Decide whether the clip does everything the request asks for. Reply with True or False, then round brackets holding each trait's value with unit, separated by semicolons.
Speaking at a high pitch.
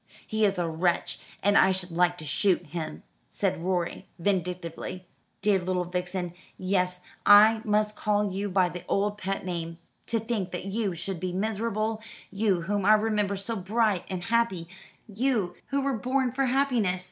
True (195 Hz)